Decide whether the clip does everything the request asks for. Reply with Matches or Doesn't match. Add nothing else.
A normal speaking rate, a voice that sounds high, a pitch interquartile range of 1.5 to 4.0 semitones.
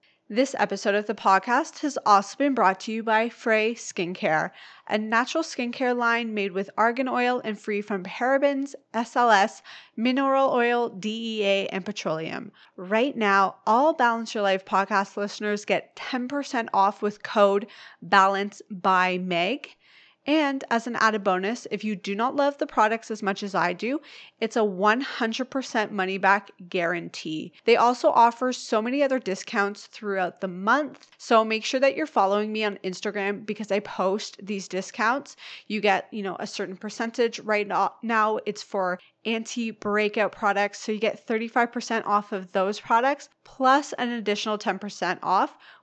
Matches